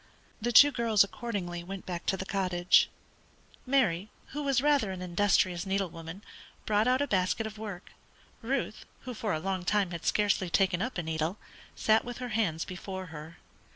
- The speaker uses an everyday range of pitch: Yes, average, 4.2 semitones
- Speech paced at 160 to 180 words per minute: Yes, average, 175 wpm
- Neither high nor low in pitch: No, high, 195 Hz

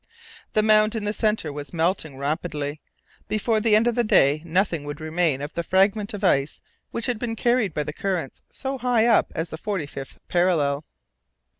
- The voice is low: No, medium, 185 Hz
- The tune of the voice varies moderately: No, wide, 6.1 semitones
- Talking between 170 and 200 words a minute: Yes, average, 190 wpm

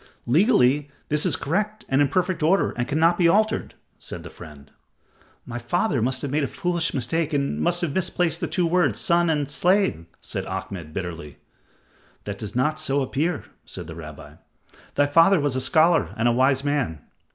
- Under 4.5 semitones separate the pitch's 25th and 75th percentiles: No, wide, 5.6 semitones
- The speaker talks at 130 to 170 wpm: No, average, 180 wpm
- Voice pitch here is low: No, medium, 145 Hz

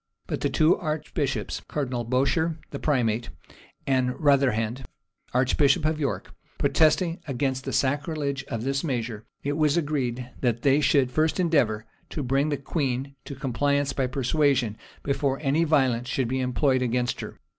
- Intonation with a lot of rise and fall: No, average, 2.9 semitones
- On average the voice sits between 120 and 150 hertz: Yes, low, 135 Hz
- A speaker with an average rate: Yes, average, 150 wpm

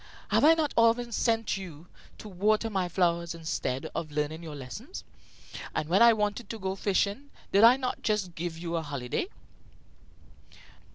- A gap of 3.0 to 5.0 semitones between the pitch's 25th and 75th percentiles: No, wide, 5.4 semitones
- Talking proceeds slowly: No, average, 165 wpm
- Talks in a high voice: Yes, high, 195 Hz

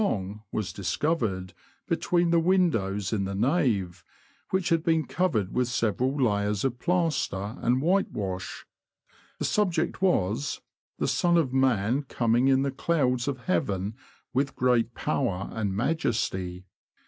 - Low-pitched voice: Yes, low, 125 Hz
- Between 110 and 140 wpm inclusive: Yes, slow, 135 wpm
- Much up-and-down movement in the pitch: Yes, wide, 7.8 semitones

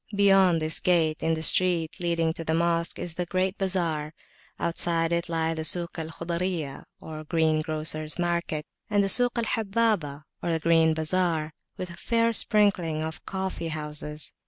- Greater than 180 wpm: No, average, 165 wpm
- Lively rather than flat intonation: No, narrow, 2.6 semitones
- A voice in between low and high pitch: Yes, medium, 165 Hz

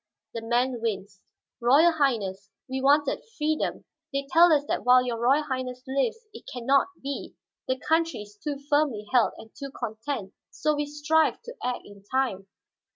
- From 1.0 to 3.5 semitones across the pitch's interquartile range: No, average, 4.2 semitones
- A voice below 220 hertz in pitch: No, very high, 265 Hz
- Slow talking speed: No, average, 170 wpm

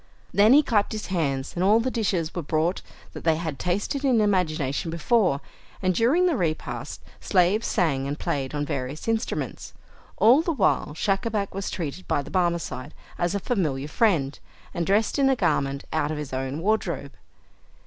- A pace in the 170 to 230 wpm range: Yes, average, 175 wpm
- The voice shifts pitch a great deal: Yes, wide, 6.4 semitones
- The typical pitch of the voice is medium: Yes, medium, 180 Hz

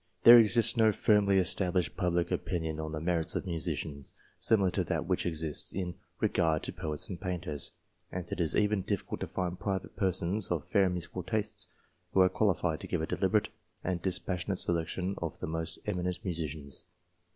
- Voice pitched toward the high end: No, very low, 90 Hz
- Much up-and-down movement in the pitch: No, average, 2.9 semitones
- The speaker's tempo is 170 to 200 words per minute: Yes, average, 180 wpm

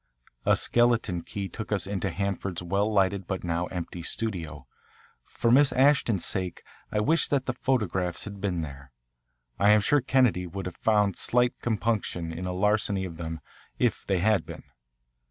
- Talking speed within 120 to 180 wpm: Yes, average, 170 wpm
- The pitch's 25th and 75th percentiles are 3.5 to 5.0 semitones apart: Yes, average, 4.0 semitones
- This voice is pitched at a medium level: No, low, 100 Hz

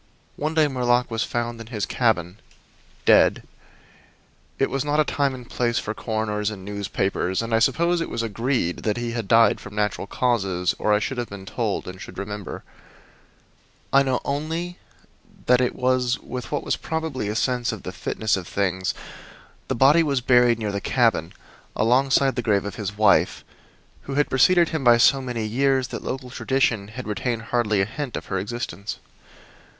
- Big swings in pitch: No, average, 4.1 semitones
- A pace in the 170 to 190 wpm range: Yes, average, 180 wpm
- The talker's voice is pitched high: No, low, 120 Hz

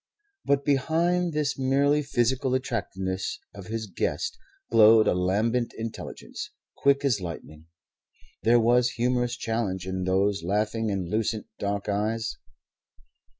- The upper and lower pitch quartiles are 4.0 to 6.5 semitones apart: Yes, average, 4.3 semitones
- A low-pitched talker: Yes, low, 115 Hz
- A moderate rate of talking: No, slow, 120 wpm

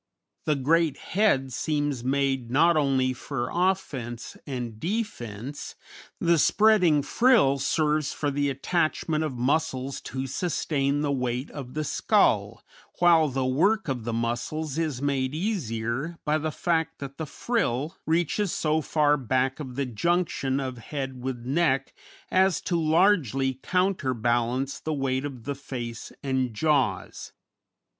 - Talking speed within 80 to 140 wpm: Yes, slow, 135 wpm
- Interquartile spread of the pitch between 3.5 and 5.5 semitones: Yes, average, 3.8 semitones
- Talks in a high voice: No, medium, 140 Hz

